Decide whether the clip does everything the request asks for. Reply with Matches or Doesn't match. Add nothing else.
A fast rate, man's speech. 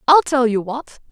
Doesn't match